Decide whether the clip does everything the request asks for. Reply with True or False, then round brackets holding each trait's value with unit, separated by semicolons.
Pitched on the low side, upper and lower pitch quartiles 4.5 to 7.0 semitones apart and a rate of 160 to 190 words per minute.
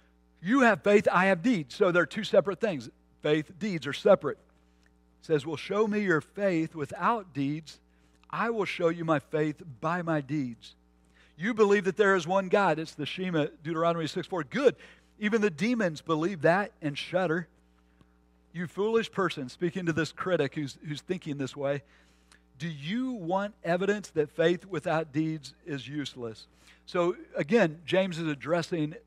False (165 Hz; 5.1 semitones; 165 wpm)